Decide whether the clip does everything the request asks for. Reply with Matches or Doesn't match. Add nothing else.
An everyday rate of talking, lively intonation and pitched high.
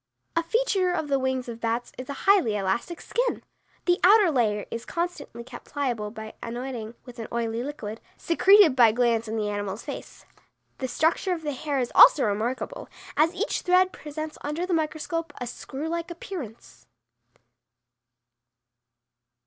Matches